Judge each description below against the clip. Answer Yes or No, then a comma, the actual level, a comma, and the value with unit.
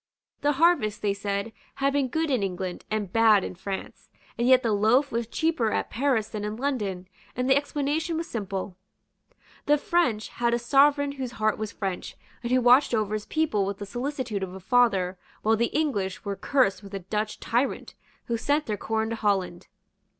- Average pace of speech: Yes, average, 195 wpm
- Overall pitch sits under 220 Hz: No, high, 225 Hz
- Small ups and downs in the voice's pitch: No, average, 5.2 semitones